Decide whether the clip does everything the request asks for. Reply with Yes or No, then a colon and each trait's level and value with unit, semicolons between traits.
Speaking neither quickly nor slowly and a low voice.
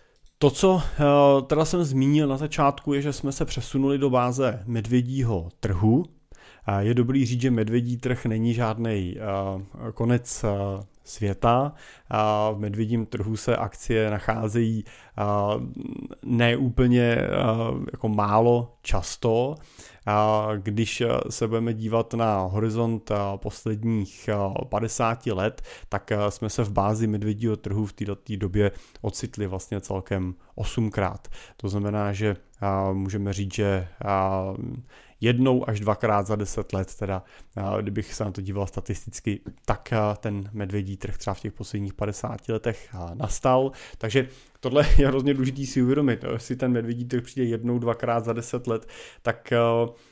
Yes: average, 130 wpm; low, 110 Hz